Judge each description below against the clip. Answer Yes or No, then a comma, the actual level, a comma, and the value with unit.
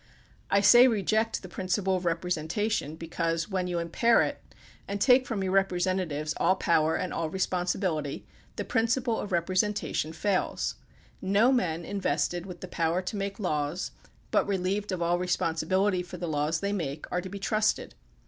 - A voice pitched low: No, medium, 185 Hz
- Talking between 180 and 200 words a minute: No, average, 165 wpm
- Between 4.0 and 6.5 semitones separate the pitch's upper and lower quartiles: No, average, 3.1 semitones